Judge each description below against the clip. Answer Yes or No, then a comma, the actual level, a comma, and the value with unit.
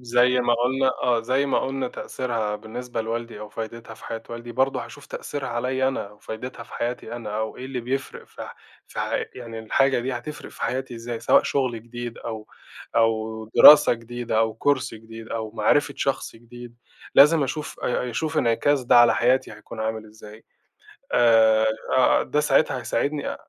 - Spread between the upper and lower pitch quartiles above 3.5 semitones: No, narrow, 2.6 semitones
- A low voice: Yes, low, 120 Hz